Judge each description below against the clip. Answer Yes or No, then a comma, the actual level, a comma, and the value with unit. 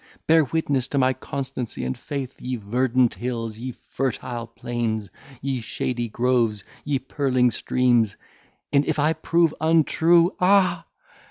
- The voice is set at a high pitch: No, low, 130 Hz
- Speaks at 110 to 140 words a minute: Yes, slow, 135 wpm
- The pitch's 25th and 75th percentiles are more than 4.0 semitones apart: No, average, 3.7 semitones